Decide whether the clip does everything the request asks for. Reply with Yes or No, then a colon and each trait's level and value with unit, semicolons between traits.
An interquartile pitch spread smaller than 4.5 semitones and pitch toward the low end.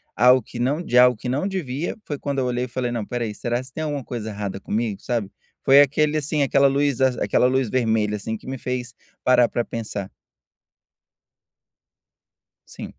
Yes: average, 3.1 semitones; low, 125 Hz